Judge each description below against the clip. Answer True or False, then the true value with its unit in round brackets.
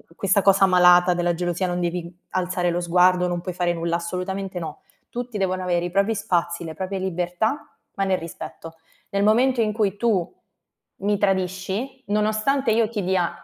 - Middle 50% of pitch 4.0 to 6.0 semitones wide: False (2.6 semitones)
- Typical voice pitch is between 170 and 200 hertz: True (185 Hz)